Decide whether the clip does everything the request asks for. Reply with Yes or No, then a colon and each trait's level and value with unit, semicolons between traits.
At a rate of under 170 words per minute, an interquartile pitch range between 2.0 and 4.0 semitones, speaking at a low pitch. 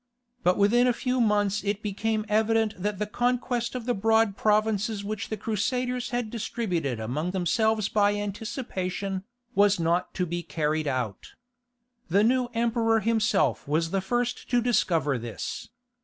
No: average, 150 wpm; average, 3.7 semitones; high, 210 Hz